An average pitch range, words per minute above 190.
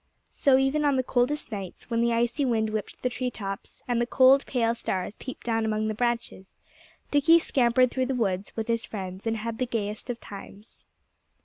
Yes: average, 3.0 semitones; average, 200 wpm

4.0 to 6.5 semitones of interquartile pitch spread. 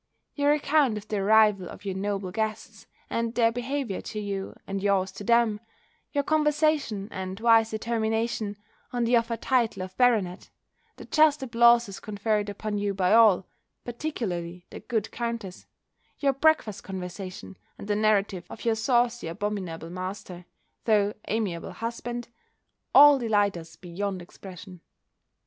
No: average, 3.4 semitones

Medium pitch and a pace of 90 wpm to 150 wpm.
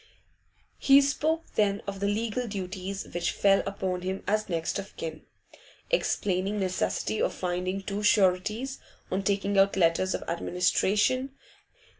No: high, 195 Hz; average, 140 wpm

